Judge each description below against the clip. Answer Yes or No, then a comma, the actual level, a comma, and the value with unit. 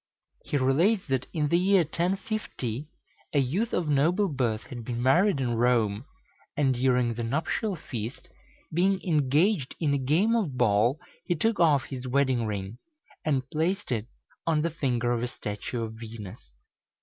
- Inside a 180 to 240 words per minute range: No, average, 160 wpm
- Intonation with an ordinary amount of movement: No, wide, 5.9 semitones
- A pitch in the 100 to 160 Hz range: Yes, low, 135 Hz